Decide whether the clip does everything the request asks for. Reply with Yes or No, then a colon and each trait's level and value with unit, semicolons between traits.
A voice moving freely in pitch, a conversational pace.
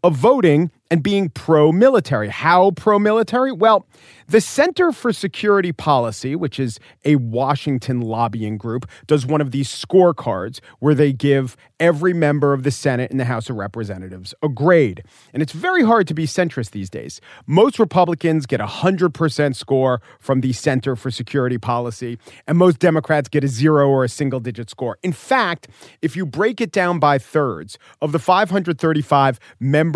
Yes: wide, 5.7 semitones; average, 170 wpm